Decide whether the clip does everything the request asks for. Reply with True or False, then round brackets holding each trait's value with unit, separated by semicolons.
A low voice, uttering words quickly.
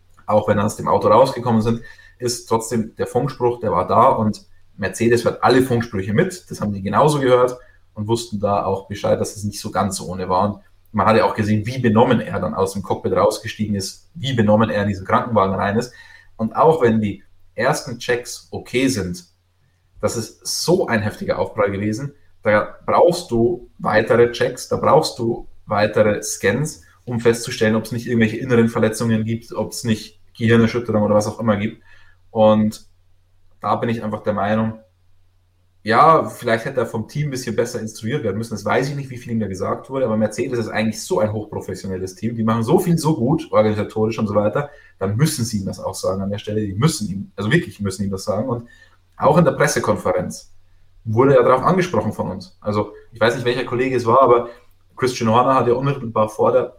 True (110 Hz; 210 wpm)